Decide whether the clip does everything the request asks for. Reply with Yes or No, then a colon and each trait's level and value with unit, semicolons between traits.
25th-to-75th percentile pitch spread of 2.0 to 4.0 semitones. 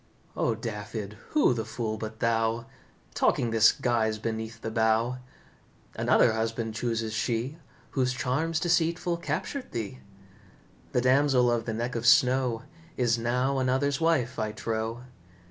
Yes: narrow, 2.5 semitones